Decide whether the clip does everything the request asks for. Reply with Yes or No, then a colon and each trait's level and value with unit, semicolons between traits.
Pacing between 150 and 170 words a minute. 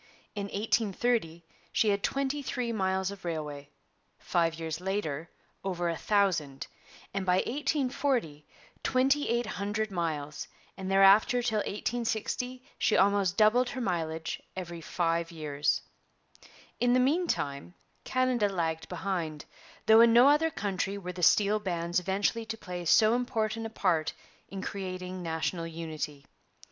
No: slow, 135 wpm